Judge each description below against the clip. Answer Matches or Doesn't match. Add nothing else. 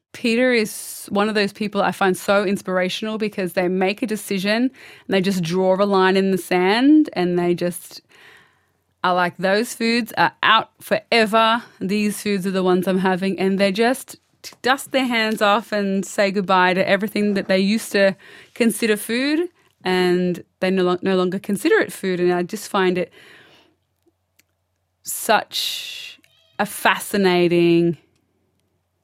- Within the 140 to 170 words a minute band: Matches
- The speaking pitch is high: Matches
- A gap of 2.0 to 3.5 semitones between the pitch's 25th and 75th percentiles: Matches